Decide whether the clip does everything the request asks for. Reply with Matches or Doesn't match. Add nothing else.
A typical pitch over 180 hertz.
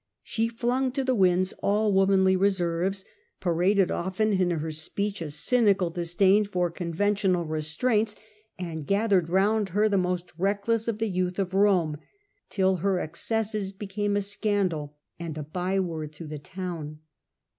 Matches